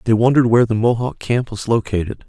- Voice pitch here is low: Yes, low, 115 Hz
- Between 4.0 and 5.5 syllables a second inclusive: No, 6.6 syllables/s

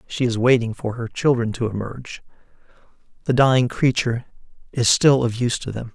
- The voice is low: Yes, low, 120 Hz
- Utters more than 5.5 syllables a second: Yes, 5.8 syllables/s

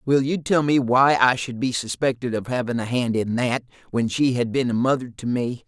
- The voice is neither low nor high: No, low, 125 Hz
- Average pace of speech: No, fast, 245 wpm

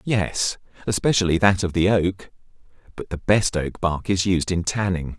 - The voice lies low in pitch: Yes, very low, 95 Hz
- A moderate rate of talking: Yes, average, 175 wpm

